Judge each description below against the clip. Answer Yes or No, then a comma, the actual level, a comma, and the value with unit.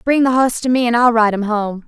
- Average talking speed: No, fast, 320 wpm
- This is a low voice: No, high, 235 Hz